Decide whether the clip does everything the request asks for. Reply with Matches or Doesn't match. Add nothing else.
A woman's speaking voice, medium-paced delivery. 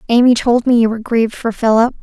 Doesn't match